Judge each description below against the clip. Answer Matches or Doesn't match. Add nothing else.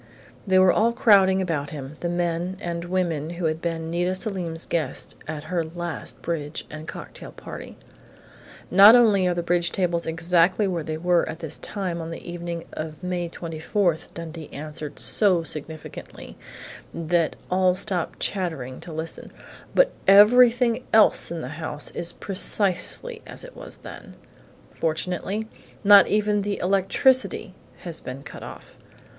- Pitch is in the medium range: Matches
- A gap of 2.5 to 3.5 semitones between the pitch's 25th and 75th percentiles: Matches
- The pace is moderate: Matches